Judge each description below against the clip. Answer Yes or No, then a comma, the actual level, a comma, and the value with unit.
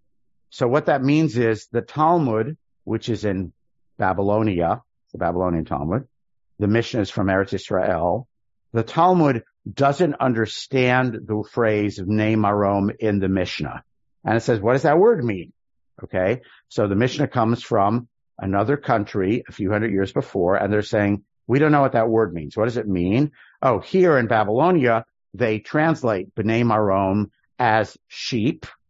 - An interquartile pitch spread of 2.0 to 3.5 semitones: No, average, 4.2 semitones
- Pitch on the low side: Yes, low, 110 Hz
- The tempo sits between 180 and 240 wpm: No, average, 155 wpm